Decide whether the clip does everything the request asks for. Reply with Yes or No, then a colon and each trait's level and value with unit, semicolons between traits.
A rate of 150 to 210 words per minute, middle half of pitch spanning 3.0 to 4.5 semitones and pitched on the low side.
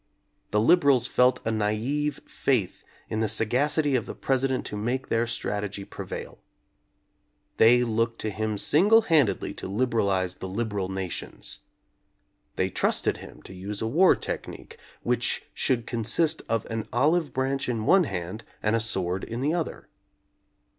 Yes: average, 155 wpm; average, 4.2 semitones; low, 115 Hz